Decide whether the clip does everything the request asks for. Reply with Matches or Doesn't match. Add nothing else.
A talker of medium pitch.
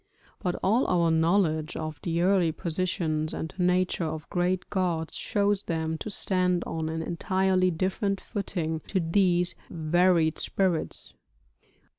Matches